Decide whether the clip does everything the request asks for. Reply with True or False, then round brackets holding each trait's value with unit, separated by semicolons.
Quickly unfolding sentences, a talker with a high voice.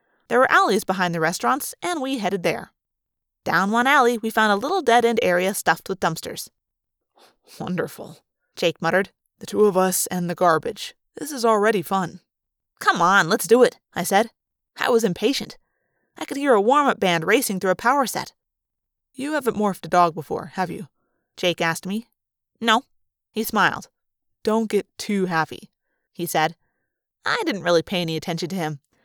False (180 wpm; 195 Hz)